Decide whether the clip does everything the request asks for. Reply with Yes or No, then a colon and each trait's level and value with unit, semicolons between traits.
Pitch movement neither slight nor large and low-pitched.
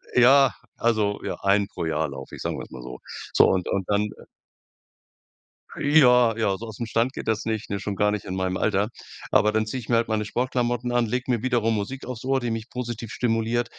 Yes: average, 3.0 semitones; low, 115 Hz